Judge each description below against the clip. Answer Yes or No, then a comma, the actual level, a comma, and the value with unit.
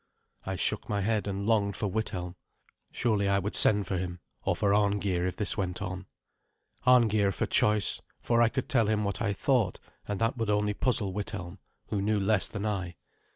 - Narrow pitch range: Yes, narrow, 2.1 semitones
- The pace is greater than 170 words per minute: Yes, average, 195 wpm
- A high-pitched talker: No, low, 100 Hz